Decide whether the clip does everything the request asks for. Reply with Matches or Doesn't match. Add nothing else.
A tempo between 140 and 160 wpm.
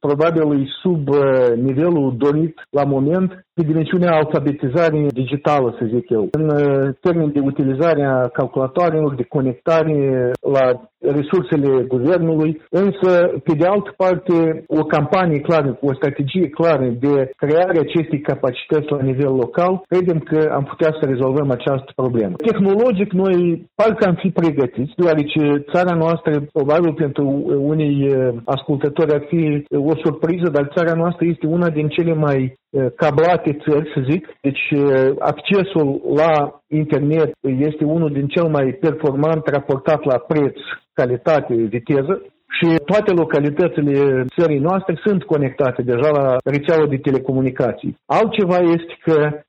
Doesn't match